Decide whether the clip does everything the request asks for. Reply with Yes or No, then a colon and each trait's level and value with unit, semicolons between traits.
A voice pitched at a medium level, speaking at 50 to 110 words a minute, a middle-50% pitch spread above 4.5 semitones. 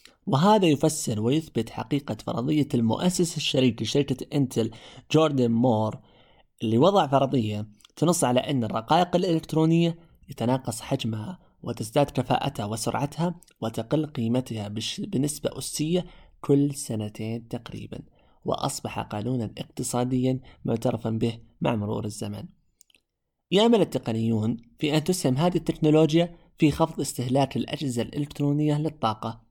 No: low, 130 Hz; average, 105 wpm; average, 5.2 semitones